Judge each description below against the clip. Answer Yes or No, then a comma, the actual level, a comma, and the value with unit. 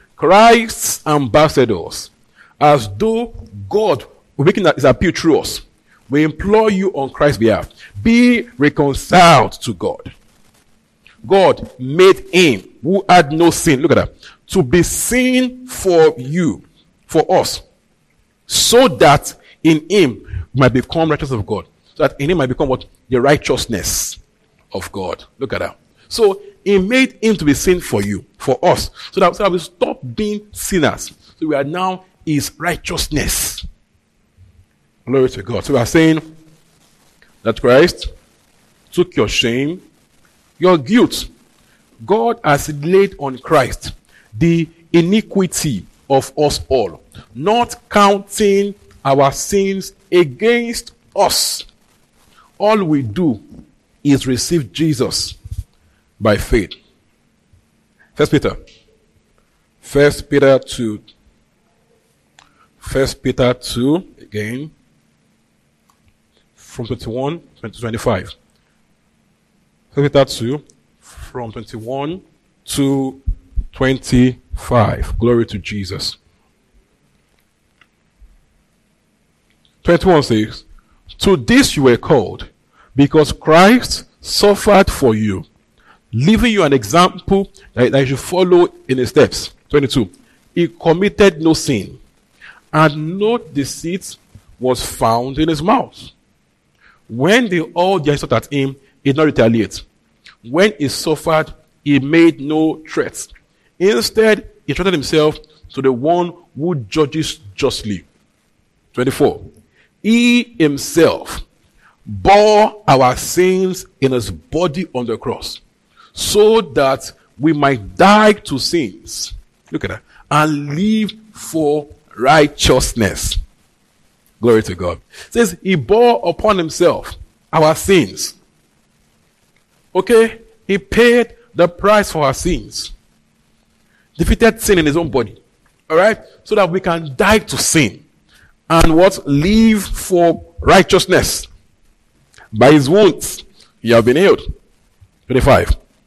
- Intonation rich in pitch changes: Yes, wide, 7.3 semitones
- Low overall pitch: No, medium, 155 Hz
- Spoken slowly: Yes, slow, 120 wpm